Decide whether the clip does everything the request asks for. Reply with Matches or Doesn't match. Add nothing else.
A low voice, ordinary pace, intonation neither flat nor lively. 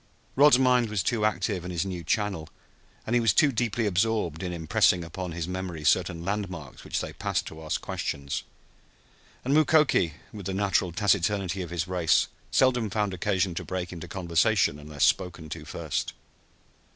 Matches